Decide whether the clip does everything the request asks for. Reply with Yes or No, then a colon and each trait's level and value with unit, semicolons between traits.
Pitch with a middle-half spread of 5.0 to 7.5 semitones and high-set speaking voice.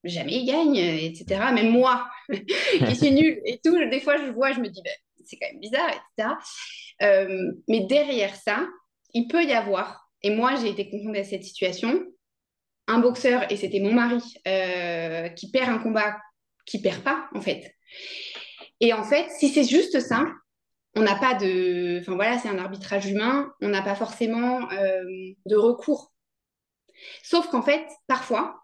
Yes: wide, 5.5 semitones; high, 230 Hz